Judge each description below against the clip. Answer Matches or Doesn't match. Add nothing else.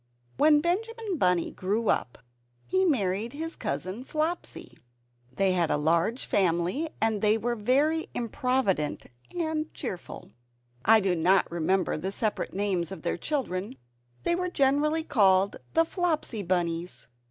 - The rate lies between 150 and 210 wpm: Doesn't match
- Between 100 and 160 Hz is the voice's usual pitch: Doesn't match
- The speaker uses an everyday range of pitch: Doesn't match